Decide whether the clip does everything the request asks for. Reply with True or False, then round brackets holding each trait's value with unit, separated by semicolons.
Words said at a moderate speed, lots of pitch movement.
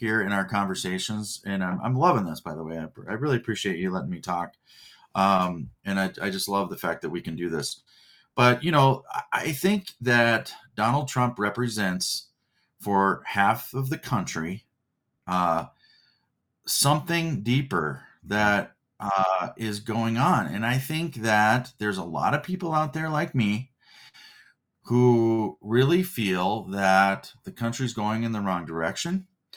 True (160 wpm; 5.7 semitones)